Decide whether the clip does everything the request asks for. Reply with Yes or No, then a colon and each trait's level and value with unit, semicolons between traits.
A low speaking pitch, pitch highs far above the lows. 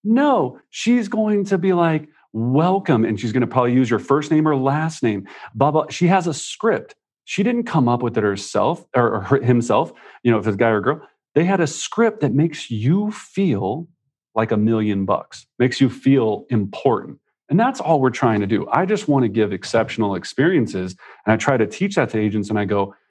Yes: low, 130 Hz; wide, 7.0 semitones